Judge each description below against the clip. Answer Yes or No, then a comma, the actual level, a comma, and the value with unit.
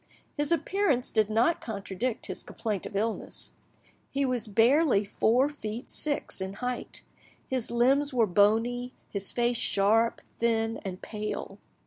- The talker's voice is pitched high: Yes, high, 230 Hz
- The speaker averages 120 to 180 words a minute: Yes, slow, 135 wpm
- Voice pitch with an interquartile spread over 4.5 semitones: No, average, 3.3 semitones